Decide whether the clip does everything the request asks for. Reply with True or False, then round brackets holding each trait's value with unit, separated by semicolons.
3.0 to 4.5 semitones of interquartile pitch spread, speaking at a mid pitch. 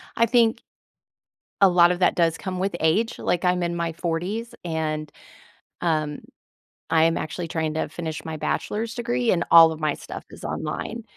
True (3.3 semitones; 170 Hz)